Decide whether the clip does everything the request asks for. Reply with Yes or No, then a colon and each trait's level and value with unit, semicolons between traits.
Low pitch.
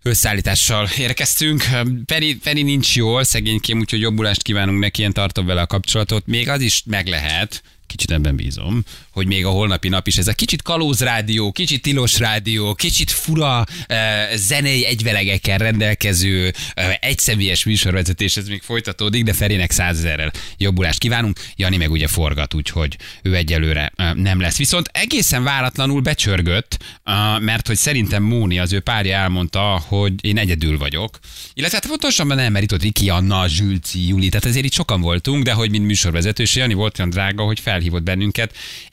Yes: low, 105 Hz